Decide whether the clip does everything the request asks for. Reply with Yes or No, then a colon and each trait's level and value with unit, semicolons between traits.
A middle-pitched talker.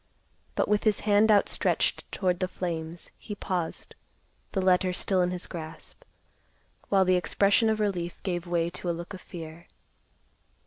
Yes: medium, 180 Hz